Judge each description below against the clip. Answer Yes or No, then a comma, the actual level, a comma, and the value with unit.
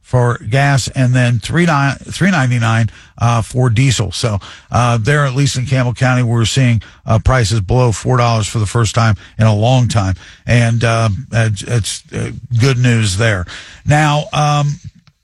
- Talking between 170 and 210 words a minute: No, average, 150 wpm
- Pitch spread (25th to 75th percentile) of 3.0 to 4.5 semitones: No, narrow, 2.5 semitones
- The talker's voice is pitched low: Yes, low, 120 Hz